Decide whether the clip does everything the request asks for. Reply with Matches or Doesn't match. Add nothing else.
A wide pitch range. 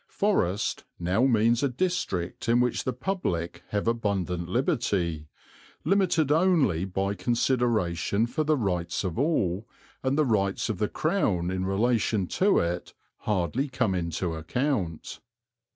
Matches